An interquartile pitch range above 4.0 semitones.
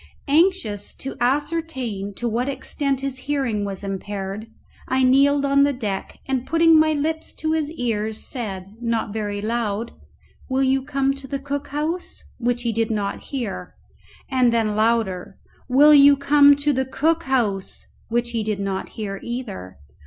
Yes: average, 4.8 semitones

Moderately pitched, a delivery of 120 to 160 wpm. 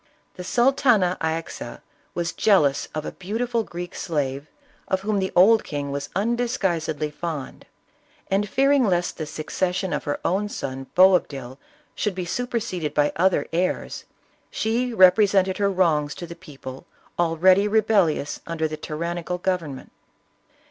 Yes: medium, 180 Hz; slow, 135 wpm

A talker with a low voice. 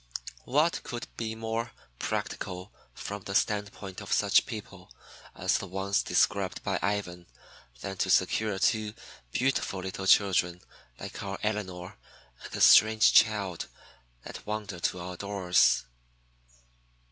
Yes: low, 100 Hz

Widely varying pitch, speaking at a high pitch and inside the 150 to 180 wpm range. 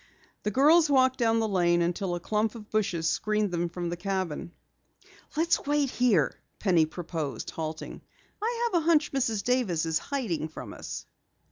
Yes: wide, 7.1 semitones; high, 210 Hz; average, 165 wpm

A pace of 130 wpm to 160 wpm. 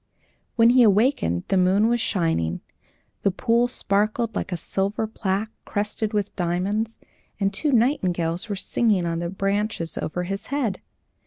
Yes: average, 150 wpm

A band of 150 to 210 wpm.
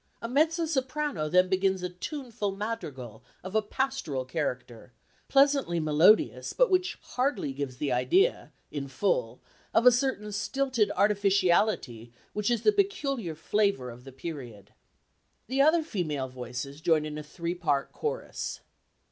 No: average, 140 wpm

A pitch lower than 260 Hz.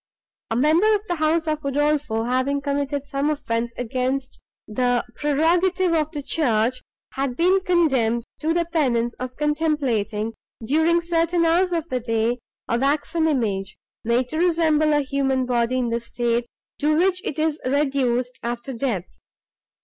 No: very high, 280 Hz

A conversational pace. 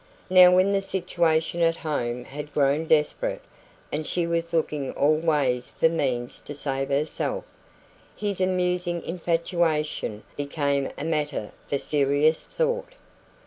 No: slow, 130 wpm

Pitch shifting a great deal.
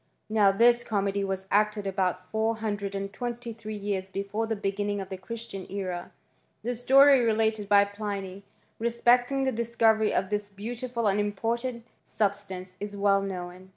No: average, 2.7 semitones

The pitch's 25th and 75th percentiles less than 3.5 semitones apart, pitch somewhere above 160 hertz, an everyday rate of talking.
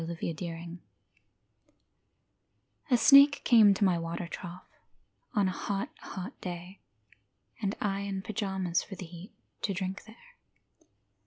No: average, 2.9 semitones; high, 190 Hz; slow, 130 wpm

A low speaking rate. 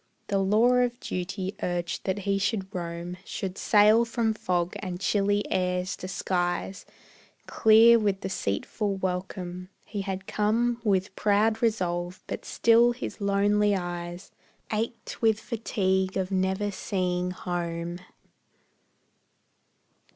Yes: slow, 120 wpm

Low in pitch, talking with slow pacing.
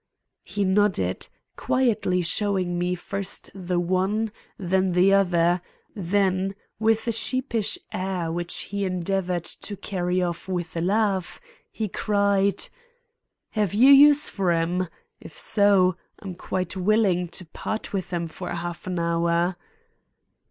No: medium, 185 Hz; slow, 130 wpm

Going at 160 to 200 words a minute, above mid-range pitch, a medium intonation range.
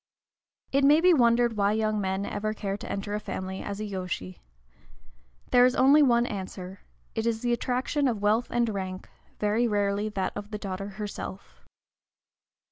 Yes: average, 165 wpm; high, 210 Hz; average, 3.2 semitones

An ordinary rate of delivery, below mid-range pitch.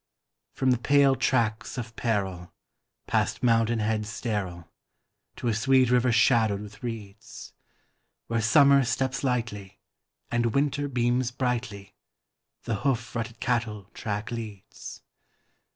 No: slow, 120 wpm; low, 115 Hz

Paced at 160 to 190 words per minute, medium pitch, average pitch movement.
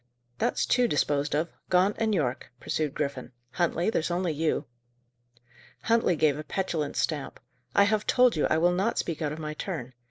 Yes: average, 180 wpm; medium, 160 Hz; average, 4.3 semitones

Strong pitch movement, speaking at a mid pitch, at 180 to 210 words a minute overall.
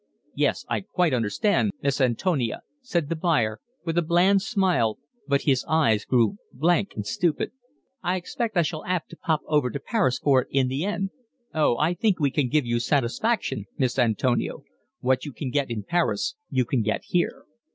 Yes: wide, 6.0 semitones; medium, 150 Hz; average, 185 wpm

